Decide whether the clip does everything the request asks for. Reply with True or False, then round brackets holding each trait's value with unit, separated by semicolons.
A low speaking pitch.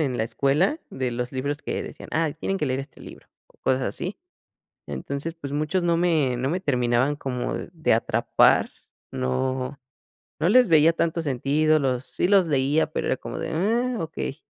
False (150 Hz)